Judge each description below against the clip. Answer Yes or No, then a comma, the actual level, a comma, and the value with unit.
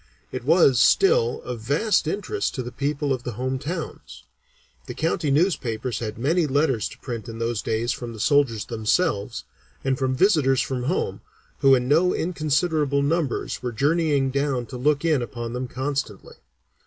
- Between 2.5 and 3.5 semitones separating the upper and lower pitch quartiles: No, average, 4.2 semitones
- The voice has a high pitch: No, low, 135 Hz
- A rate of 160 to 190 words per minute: Yes, average, 165 wpm